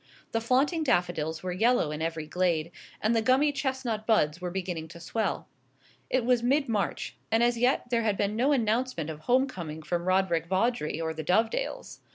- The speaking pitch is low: No, high, 210 Hz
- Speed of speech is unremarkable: Yes, average, 190 wpm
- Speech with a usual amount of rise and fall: No, wide, 6.5 semitones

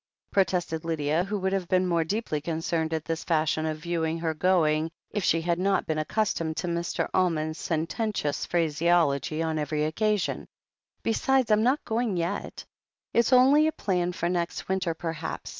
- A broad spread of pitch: No, average, 3.3 semitones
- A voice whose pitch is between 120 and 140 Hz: No, medium, 170 Hz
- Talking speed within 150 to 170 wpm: Yes, average, 165 wpm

